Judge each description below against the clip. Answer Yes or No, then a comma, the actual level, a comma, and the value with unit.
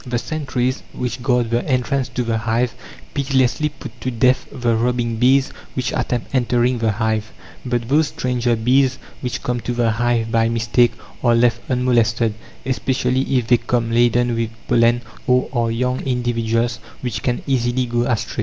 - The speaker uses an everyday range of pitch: No, narrow, 1.5 semitones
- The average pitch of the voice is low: Yes, low, 120 Hz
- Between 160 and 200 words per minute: Yes, average, 165 wpm